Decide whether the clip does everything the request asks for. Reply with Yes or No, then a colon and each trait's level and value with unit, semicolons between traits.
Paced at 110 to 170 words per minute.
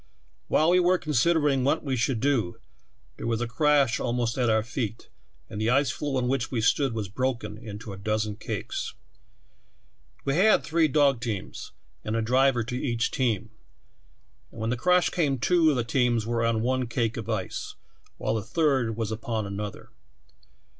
No: average, 180 wpm